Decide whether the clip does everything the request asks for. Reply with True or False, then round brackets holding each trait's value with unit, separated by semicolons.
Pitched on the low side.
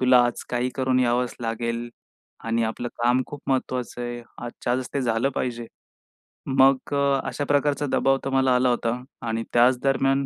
True (125 Hz)